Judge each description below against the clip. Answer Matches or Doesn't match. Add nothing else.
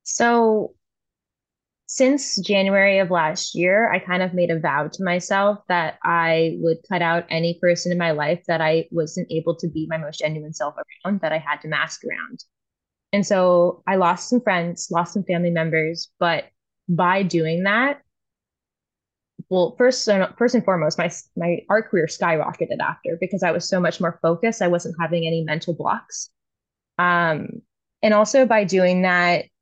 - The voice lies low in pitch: Doesn't match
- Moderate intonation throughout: Matches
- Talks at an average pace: Matches